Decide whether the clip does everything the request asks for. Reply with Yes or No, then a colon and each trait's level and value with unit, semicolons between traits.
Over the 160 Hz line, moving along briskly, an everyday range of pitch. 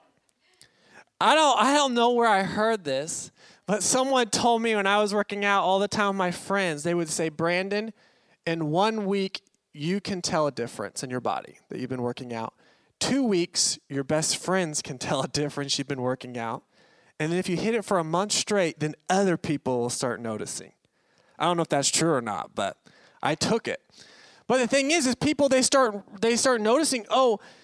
No: high, 190 Hz; fast, 210 wpm; wide, 6.8 semitones